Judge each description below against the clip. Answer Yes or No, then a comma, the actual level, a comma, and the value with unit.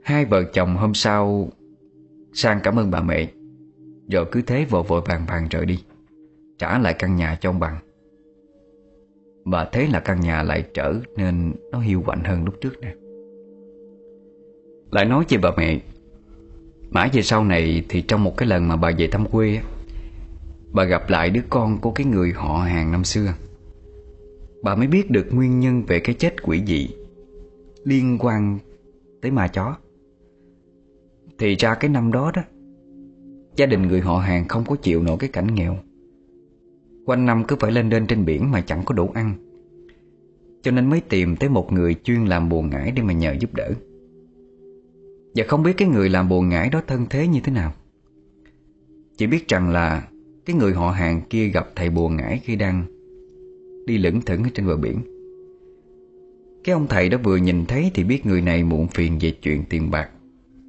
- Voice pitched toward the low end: Yes, low, 105 Hz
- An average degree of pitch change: No, wide, 8.8 semitones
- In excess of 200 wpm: No, average, 185 wpm